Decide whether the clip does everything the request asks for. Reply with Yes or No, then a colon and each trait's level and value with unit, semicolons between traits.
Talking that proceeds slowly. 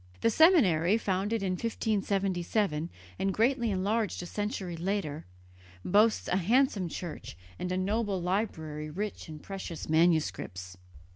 Yes: slow, 125 wpm